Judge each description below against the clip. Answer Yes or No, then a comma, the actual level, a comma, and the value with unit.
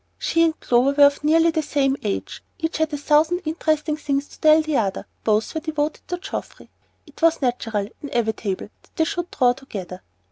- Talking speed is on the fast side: No, average, 190 wpm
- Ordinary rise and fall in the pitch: Yes, average, 4.5 semitones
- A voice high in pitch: Yes, very high, 295 Hz